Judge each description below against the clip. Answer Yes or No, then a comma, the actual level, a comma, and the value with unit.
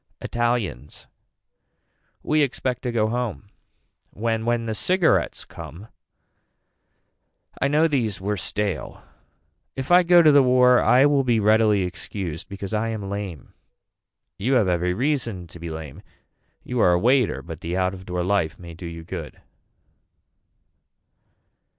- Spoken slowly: No, average, 145 wpm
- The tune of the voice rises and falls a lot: Yes, wide, 5.8 semitones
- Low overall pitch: Yes, low, 110 Hz